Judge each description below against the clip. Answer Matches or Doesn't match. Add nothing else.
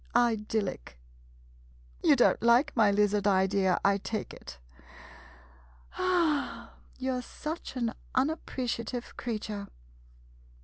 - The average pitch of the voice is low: Doesn't match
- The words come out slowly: Matches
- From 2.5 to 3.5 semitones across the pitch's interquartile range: Doesn't match